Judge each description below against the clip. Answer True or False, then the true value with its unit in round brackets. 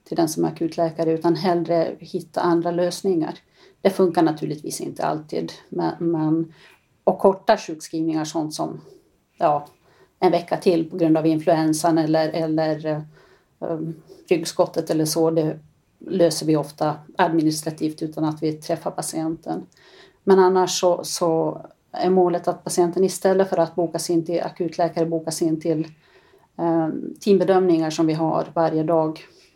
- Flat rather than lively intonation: True (1.8 semitones)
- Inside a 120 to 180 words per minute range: True (145 wpm)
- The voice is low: False (165 Hz)